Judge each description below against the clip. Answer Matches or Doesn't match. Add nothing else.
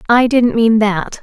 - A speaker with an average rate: Matches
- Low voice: Doesn't match